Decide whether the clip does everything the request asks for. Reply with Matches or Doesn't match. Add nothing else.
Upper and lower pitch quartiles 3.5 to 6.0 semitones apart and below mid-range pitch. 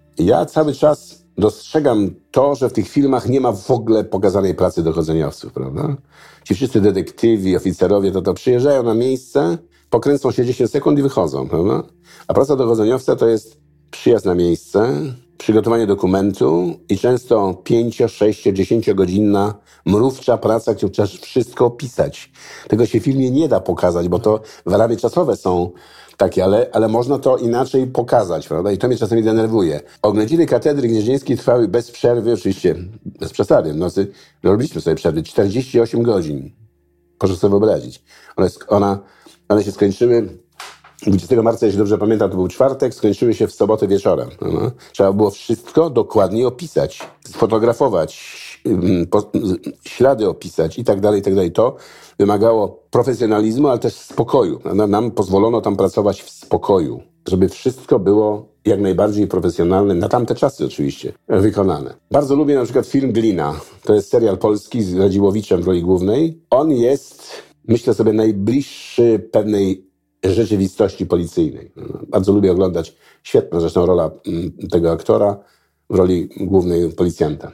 Matches